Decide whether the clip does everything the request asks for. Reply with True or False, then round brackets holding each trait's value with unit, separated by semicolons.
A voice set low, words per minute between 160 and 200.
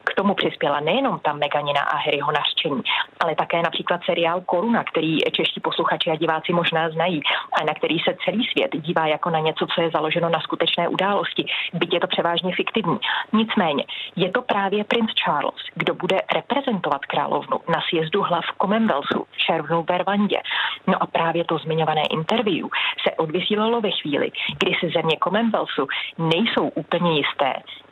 False (170 Hz; 165 wpm)